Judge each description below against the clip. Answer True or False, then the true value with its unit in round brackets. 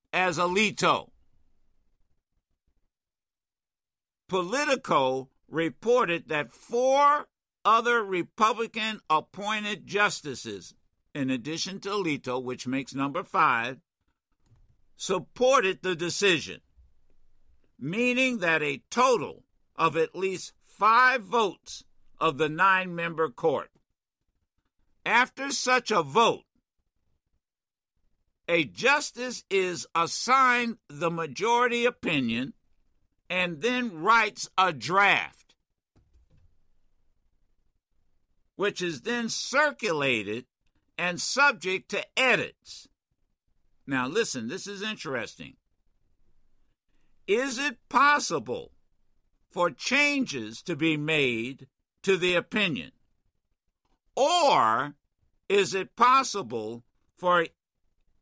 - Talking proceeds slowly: True (80 wpm)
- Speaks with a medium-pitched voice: True (180 Hz)